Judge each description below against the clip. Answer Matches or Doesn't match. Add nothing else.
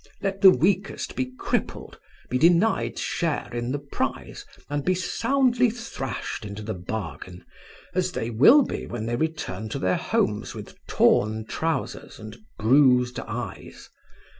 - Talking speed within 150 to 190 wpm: Doesn't match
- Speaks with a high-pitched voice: Doesn't match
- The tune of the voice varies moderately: Doesn't match